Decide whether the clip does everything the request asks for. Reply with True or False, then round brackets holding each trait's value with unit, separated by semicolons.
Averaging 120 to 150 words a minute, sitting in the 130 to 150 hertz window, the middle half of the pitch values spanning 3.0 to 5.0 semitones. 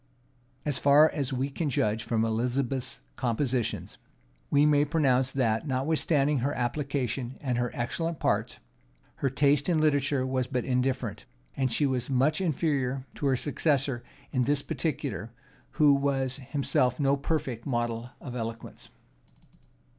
False (135 wpm; 135 Hz; 2.6 semitones)